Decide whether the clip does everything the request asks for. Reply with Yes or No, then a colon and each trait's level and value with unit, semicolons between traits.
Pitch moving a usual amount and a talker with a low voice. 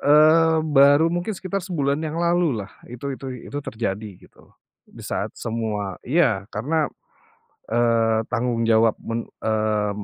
No: wide, 6.2 semitones; low, 125 Hz